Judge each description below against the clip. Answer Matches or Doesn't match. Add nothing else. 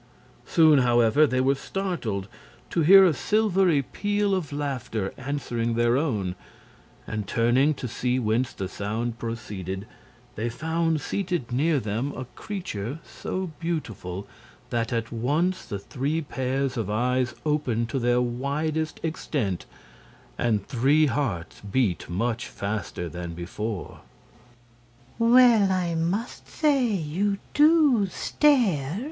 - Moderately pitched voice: Doesn't match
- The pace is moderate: Doesn't match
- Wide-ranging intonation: Matches